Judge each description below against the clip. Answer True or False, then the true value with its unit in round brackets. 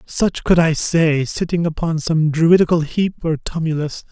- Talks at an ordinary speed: True (160 wpm)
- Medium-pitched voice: True (160 Hz)